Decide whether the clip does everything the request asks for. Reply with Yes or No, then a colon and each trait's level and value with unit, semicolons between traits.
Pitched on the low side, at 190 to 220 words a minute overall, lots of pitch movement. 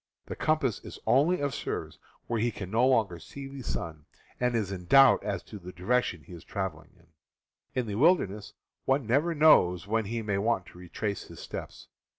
Yes: low, 110 Hz; average, 200 wpm; wide, 5.9 semitones